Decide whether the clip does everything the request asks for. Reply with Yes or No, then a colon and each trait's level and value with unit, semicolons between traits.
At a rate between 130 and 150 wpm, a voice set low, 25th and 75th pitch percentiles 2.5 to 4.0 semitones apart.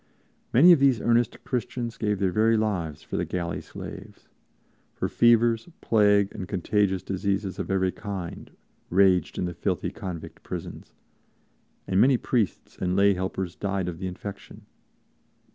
Yes: average, 145 wpm; low, 100 Hz; average, 3.4 semitones